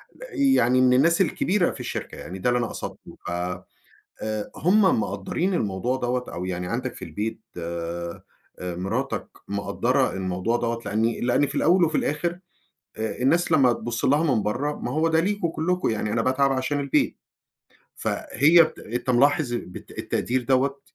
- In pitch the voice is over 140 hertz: No, low, 125 Hz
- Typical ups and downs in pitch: No, wide, 6.3 semitones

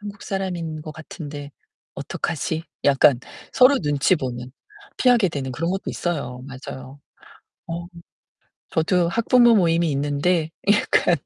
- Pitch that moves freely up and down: No, average, 4.6 semitones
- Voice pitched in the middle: Yes, medium, 160 Hz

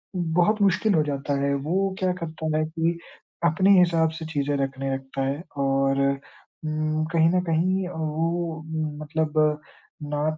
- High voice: No, medium, 160 Hz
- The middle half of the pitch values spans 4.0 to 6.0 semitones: No, average, 2.8 semitones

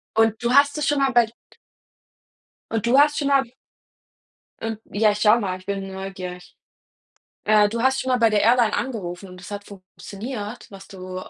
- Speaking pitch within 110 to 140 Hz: No, high, 215 Hz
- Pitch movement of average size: Yes, average, 4.2 semitones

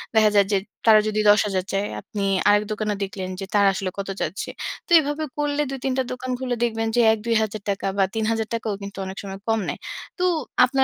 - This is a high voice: Yes, high, 215 Hz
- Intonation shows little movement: No, average, 3.3 semitones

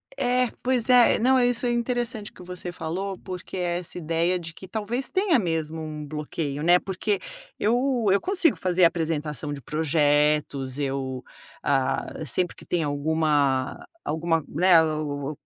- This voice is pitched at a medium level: Yes, medium, 165 Hz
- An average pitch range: No, wide, 5.7 semitones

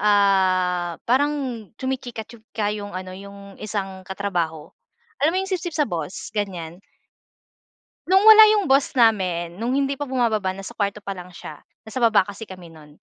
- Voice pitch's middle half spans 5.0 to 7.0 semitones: Yes, wide, 5.4 semitones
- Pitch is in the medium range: No, high, 205 Hz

